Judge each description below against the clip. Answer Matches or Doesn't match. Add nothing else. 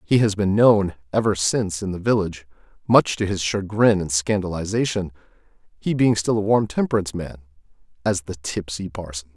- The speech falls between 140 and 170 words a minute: Matches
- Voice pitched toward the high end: Doesn't match